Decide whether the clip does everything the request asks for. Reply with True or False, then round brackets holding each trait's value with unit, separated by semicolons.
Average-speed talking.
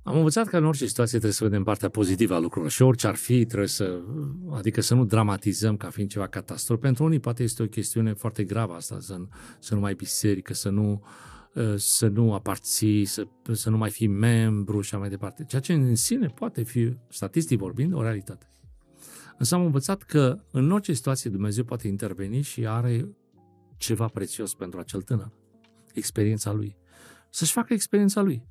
False (190 wpm)